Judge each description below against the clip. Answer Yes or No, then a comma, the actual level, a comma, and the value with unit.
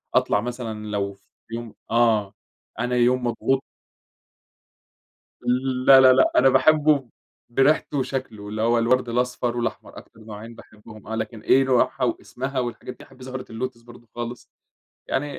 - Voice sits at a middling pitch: No, low, 120 Hz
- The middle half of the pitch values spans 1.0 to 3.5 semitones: Yes, narrow, 2.5 semitones